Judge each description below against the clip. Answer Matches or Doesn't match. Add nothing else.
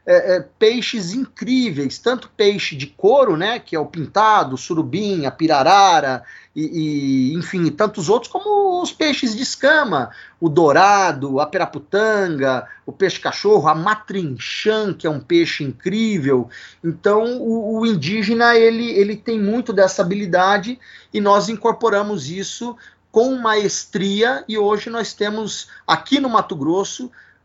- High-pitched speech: Matches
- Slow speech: Doesn't match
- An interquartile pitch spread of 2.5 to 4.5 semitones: Doesn't match